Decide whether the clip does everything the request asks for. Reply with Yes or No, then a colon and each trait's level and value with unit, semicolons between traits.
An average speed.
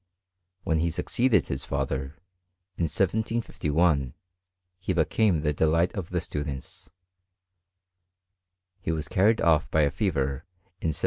No: slow, 125 wpm